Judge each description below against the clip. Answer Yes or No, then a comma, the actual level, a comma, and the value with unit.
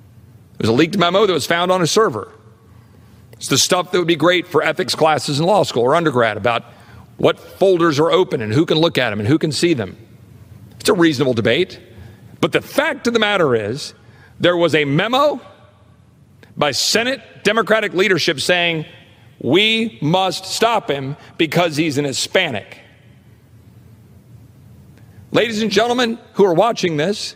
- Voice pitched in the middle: Yes, medium, 155 Hz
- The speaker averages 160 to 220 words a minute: Yes, average, 170 wpm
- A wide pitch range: Yes, wide, 8.3 semitones